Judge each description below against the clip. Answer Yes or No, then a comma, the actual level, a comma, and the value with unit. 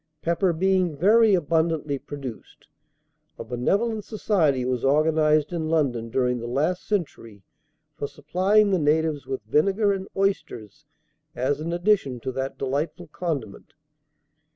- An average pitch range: No, wide, 5.7 semitones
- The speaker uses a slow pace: Yes, slow, 130 wpm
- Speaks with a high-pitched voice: No, medium, 155 Hz